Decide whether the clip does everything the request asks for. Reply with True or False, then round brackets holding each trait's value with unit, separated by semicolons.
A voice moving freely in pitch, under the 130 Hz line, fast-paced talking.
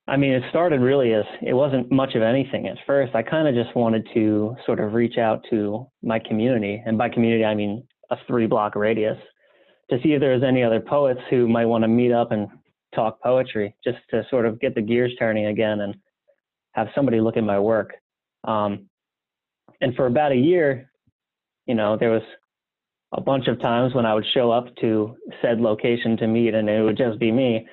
False (2.4 semitones; 115 Hz; 210 wpm)